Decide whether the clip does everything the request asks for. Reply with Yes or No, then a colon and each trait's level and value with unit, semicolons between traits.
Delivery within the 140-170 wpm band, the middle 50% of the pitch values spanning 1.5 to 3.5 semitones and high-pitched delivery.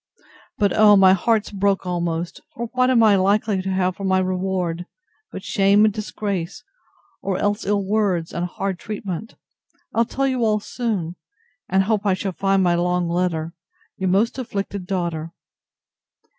Yes: average, 160 wpm; average, 2.8 semitones; high, 195 Hz